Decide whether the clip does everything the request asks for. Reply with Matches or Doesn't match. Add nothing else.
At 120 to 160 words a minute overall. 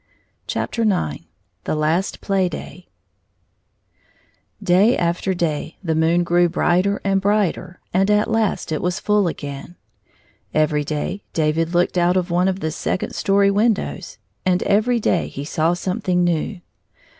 Matches